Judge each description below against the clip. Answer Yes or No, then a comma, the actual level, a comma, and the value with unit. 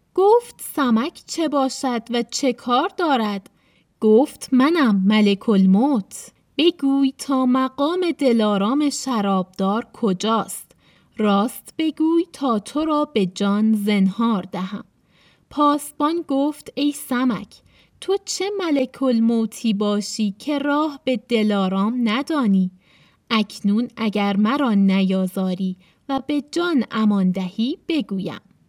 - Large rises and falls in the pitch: Yes, wide, 5.7 semitones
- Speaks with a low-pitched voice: No, high, 235 Hz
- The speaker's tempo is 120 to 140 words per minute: No, slow, 105 wpm